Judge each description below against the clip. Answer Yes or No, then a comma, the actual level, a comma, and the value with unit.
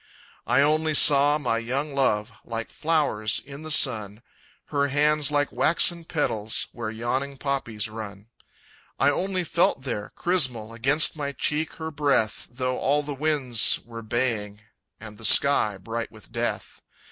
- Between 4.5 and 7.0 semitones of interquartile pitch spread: Yes, average, 4.8 semitones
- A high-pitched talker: No, low, 135 Hz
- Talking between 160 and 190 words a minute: No, average, 145 wpm